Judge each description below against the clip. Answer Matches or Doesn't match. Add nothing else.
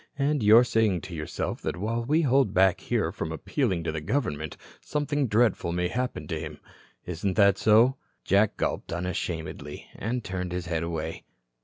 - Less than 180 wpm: Matches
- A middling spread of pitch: Doesn't match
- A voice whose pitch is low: Matches